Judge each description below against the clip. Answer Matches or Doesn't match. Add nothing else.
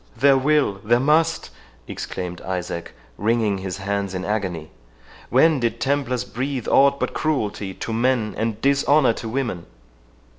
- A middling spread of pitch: Doesn't match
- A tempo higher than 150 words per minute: Doesn't match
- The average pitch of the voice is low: Matches